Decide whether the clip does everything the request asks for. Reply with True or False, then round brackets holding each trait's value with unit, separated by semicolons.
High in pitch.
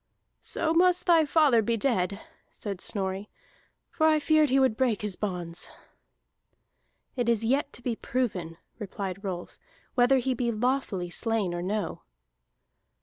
True (230 Hz)